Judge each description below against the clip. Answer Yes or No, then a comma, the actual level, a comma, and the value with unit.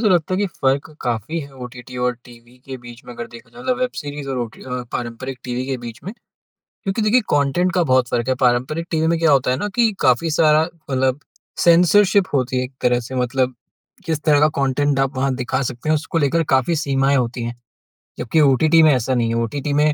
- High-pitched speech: No, low, 135 Hz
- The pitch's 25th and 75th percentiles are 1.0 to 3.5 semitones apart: No, average, 4.2 semitones